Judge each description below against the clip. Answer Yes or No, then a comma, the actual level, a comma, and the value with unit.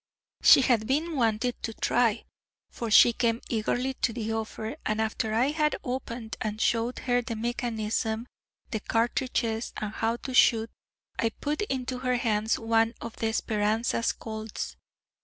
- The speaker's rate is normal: Yes, average, 155 wpm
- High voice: Yes, high, 230 Hz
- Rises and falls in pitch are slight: Yes, narrow, 2.0 semitones